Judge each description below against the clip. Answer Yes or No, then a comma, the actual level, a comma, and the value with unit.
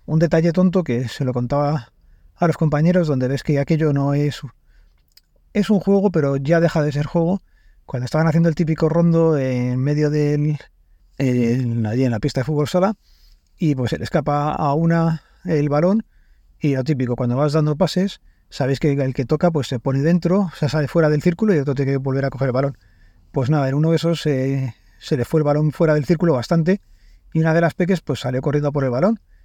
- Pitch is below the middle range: No, medium, 150 Hz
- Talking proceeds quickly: Yes, fast, 215 wpm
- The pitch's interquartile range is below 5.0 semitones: Yes, average, 4.2 semitones